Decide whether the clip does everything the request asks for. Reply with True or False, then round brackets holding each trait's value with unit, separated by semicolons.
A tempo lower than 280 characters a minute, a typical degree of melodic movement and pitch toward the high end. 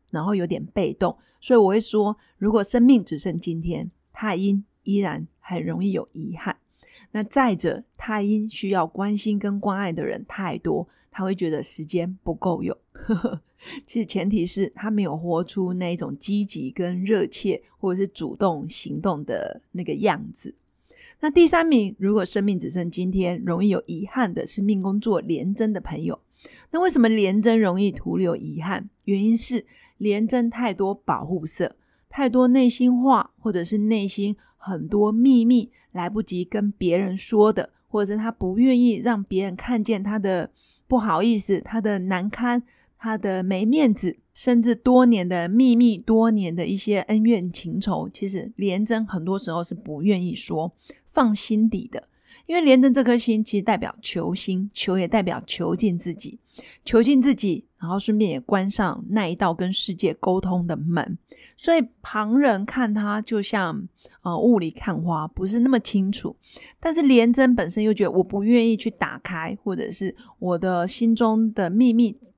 True (250 characters per minute; 3.7 semitones; 205 Hz)